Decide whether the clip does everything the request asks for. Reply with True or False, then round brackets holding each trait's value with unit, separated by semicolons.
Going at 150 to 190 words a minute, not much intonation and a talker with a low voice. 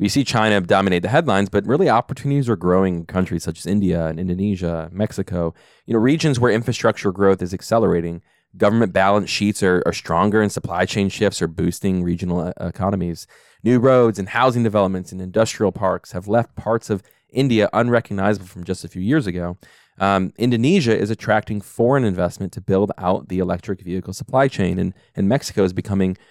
False (180 wpm; 3.7 semitones; 100 Hz)